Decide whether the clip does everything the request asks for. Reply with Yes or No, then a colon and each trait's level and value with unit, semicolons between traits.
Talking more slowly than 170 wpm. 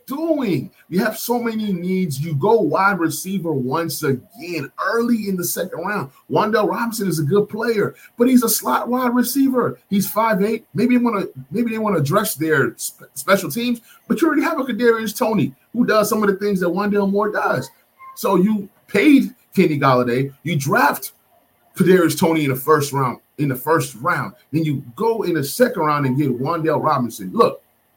No: average, 195 wpm